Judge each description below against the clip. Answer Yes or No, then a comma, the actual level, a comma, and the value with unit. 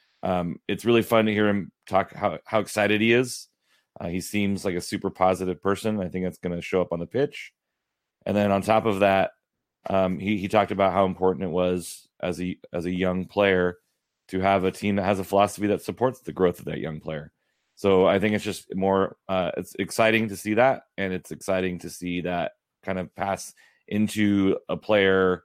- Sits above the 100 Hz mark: No, very low, 95 Hz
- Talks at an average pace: No, fast, 215 wpm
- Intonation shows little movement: Yes, narrow, 2.3 semitones